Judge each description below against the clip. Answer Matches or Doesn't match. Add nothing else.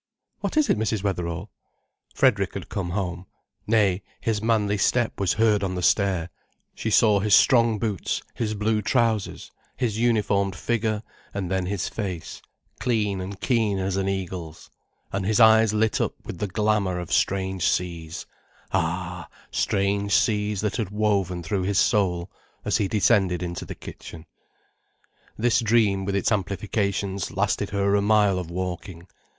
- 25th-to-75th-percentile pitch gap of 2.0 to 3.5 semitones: Matches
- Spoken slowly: Doesn't match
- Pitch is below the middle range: Matches